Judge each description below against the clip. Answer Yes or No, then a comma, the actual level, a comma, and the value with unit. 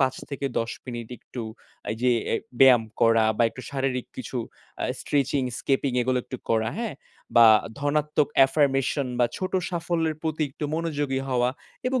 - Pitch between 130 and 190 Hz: Yes, low, 135 Hz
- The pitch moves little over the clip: No, average, 3.2 semitones